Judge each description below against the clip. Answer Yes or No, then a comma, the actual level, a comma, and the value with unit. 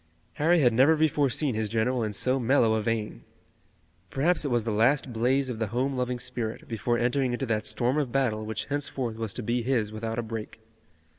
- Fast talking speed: Yes, fast, 210 wpm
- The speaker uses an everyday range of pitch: Yes, average, 3.2 semitones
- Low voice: Yes, low, 120 Hz